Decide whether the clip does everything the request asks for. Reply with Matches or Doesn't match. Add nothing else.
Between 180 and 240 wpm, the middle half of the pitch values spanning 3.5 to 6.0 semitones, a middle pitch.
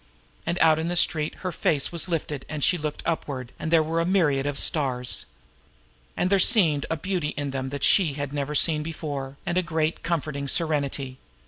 Doesn't match